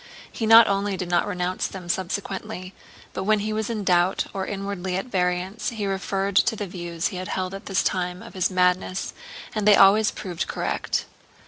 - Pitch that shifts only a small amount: Yes, narrow, 2.2 semitones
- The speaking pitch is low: No, high, 195 Hz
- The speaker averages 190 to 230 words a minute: Yes, average, 195 wpm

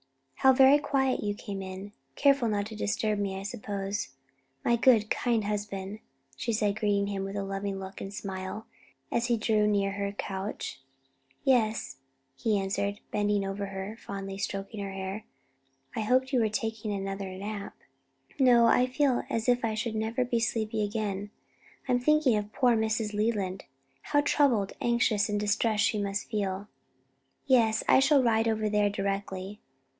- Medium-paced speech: Yes, average, 165 wpm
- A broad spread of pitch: No, narrow, 2.6 semitones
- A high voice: Yes, high, 210 Hz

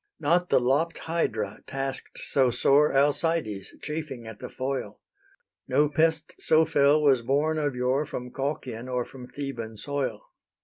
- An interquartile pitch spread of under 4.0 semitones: Yes, average, 3.5 semitones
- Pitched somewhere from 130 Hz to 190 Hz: Yes, medium, 140 Hz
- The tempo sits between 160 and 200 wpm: No, average, 145 wpm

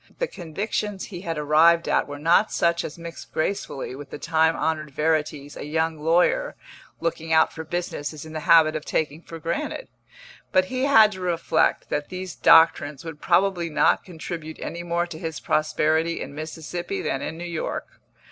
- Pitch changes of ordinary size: No, narrow, 2.0 semitones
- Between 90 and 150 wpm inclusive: No, average, 180 wpm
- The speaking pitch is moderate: Yes, medium, 165 Hz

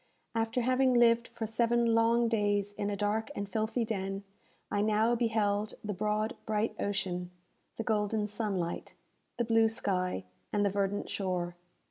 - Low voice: No, high, 215 Hz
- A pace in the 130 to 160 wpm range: Yes, average, 150 wpm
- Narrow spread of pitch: Yes, narrow, 2.1 semitones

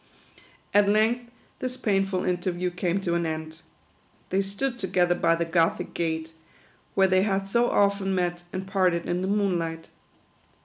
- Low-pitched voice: No, medium, 185 Hz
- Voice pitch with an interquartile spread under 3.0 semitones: Yes, narrow, 2.6 semitones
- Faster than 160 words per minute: No, average, 150 wpm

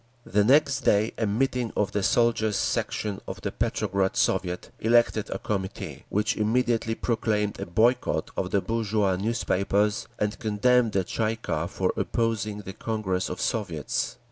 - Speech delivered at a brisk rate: No, average, 155 wpm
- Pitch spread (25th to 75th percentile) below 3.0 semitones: Yes, narrow, 2.6 semitones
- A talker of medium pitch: No, low, 105 Hz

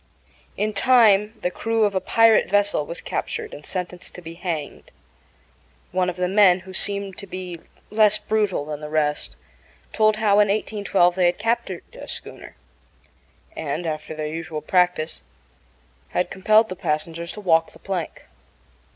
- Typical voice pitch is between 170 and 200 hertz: Yes, medium, 185 Hz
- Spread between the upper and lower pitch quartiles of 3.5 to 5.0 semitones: Yes, average, 4.0 semitones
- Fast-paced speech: No, average, 160 wpm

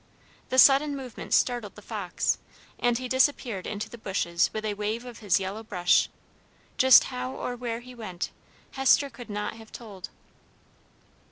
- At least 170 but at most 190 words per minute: No, average, 160 wpm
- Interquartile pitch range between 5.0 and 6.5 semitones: No, average, 3.6 semitones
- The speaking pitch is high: Yes, high, 225 Hz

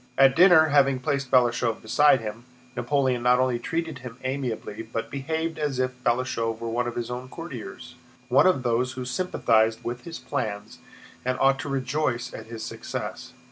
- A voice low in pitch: Yes, low, 125 Hz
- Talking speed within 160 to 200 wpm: Yes, average, 175 wpm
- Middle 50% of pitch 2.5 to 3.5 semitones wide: Yes, average, 2.9 semitones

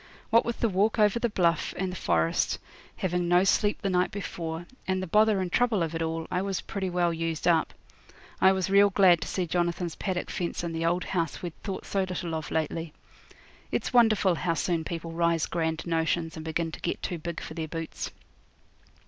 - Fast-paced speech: Yes, fast, 210 wpm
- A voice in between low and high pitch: Yes, medium, 175 Hz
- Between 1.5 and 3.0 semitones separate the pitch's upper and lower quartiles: Yes, narrow, 2.6 semitones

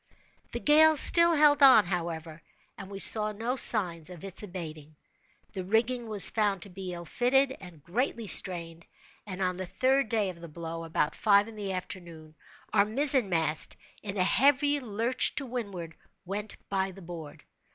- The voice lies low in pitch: No, high, 195 Hz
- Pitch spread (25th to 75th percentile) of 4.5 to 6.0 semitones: Yes, wide, 5.4 semitones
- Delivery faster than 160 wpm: Yes, average, 170 wpm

